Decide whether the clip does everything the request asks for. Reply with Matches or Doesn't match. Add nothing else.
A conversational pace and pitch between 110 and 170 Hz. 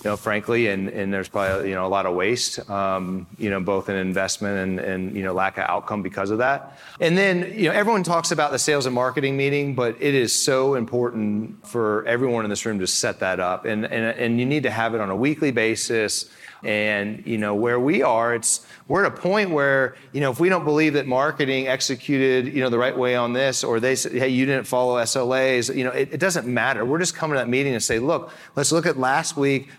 Doesn't match